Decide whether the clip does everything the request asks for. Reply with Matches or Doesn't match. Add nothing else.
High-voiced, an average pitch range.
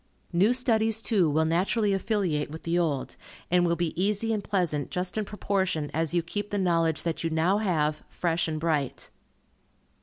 Doesn't match